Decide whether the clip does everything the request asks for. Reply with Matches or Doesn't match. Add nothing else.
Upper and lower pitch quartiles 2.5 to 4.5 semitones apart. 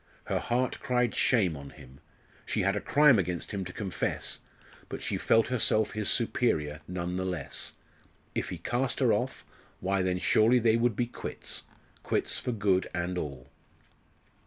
Doesn't match